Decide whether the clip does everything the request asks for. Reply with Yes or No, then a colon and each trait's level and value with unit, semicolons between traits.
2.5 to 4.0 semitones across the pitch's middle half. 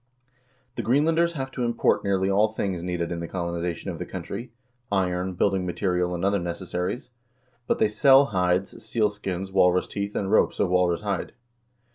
Yes: average, 3.1 semitones